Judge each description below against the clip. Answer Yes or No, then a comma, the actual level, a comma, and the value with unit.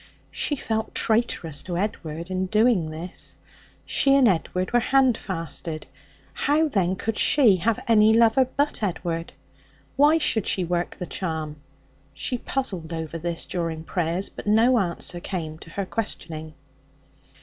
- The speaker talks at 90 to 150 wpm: Yes, average, 140 wpm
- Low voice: No, medium, 185 Hz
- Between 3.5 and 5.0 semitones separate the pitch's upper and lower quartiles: No, wide, 5.6 semitones